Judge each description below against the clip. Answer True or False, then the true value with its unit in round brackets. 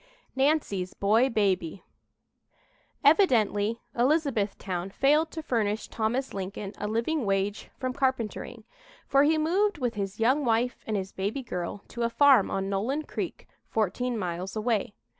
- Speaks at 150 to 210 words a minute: False (140 wpm)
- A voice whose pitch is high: True (225 Hz)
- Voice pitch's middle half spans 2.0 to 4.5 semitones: False (5.2 semitones)